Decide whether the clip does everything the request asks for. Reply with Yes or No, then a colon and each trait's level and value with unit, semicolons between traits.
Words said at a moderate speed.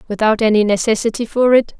Yes: average, 165 wpm